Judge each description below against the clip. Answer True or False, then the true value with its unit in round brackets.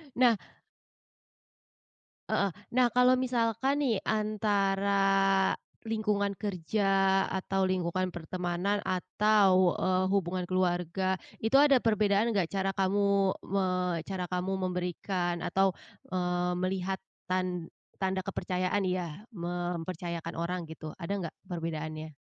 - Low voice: False (190 Hz)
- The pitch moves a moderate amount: False (2.2 semitones)